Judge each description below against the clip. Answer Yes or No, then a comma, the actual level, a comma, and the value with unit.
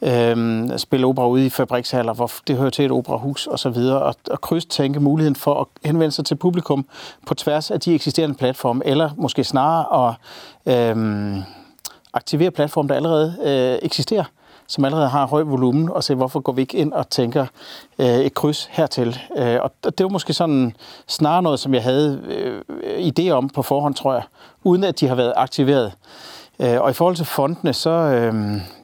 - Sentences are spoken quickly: No, average, 185 wpm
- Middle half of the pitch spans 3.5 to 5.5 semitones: Yes, average, 3.8 semitones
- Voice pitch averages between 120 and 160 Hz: Yes, medium, 140 Hz